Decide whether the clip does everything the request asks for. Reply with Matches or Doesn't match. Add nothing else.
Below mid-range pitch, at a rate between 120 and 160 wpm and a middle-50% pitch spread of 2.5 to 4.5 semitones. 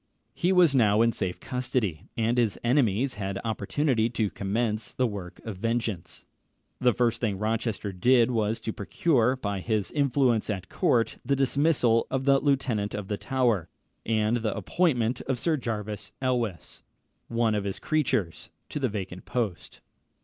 Matches